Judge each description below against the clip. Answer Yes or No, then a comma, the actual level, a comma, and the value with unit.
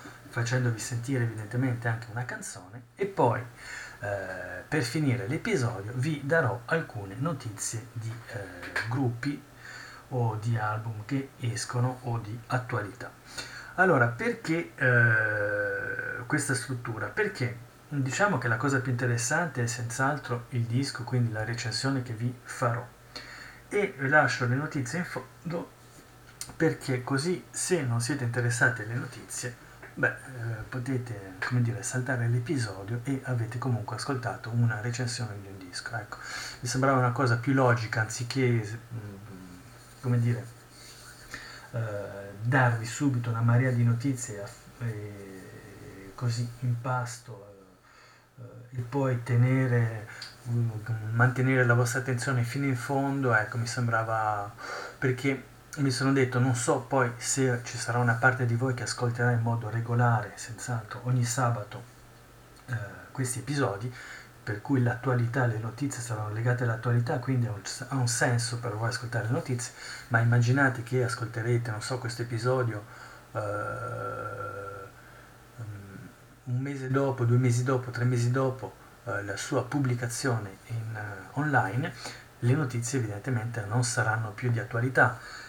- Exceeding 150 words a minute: No, average, 135 wpm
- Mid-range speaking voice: No, low, 120 Hz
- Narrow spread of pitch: Yes, narrow, 1.8 semitones